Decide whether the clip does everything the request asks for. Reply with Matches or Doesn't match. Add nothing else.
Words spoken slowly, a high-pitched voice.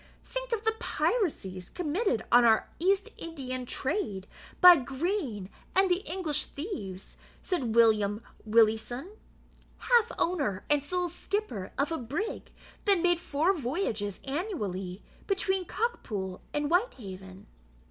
Matches